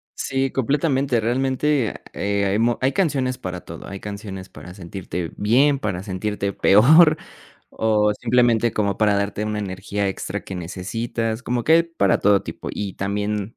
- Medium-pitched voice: No, low, 105 Hz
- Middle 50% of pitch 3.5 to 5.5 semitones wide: Yes, average, 4.4 semitones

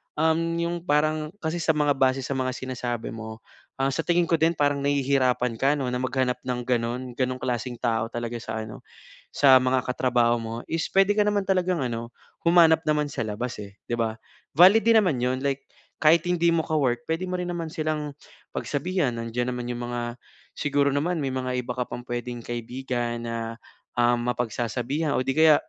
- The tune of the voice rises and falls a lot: No, average, 4.5 semitones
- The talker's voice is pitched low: Yes, low, 130 Hz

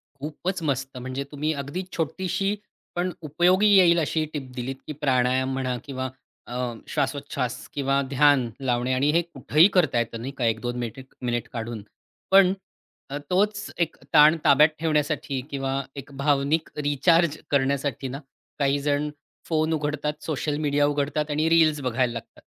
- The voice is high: No, medium, 145 Hz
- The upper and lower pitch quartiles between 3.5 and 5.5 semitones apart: No, average, 3.1 semitones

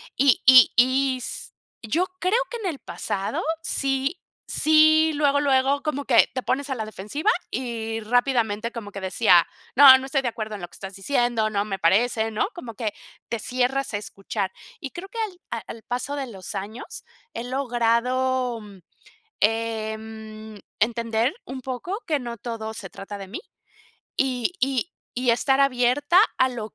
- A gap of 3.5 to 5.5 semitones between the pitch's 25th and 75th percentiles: Yes, average, 3.8 semitones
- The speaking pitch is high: Yes, high, 245 Hz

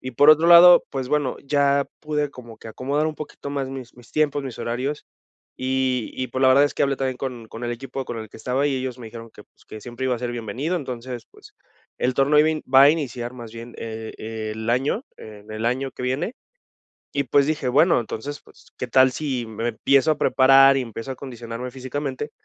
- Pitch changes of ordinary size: Yes, average, 3.1 semitones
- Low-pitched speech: Yes, low, 130 Hz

